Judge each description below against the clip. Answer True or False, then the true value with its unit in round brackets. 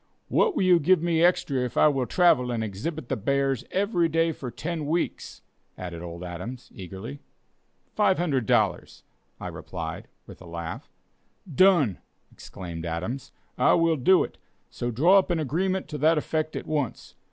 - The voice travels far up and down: True (7.1 semitones)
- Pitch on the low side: False (145 Hz)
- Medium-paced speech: True (165 wpm)